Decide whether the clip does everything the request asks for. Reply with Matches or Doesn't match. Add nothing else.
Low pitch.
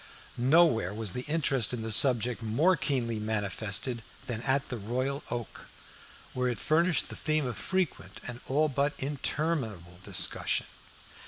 Matches